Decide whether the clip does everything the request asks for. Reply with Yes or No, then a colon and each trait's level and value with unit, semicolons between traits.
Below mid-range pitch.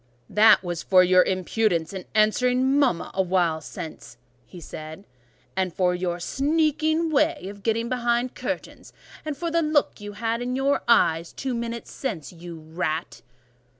No: high, 215 Hz